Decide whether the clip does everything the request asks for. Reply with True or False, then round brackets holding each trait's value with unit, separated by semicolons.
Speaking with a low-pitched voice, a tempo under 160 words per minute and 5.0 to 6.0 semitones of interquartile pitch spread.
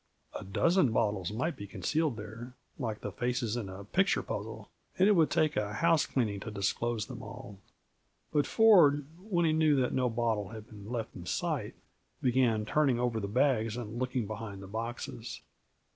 False (120 Hz; 175 wpm; 5.3 semitones)